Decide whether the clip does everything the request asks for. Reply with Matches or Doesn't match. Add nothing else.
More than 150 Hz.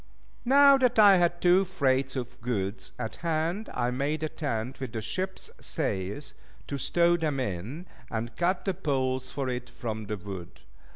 Doesn't match